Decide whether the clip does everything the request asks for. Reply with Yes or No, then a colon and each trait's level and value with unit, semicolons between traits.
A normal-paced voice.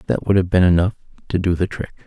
No: fast, 260 wpm